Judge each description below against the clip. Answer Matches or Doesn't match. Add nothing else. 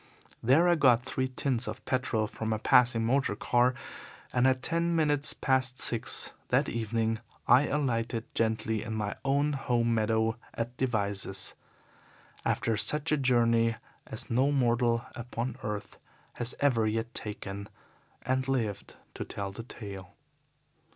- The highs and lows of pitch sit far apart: Doesn't match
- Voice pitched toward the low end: Matches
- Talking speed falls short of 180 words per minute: Matches